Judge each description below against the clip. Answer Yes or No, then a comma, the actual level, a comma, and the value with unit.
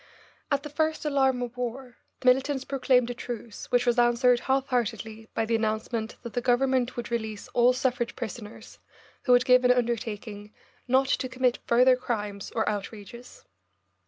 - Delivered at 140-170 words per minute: Yes, average, 165 wpm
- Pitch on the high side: Yes, high, 245 Hz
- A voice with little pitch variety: Yes, narrow, 2.2 semitones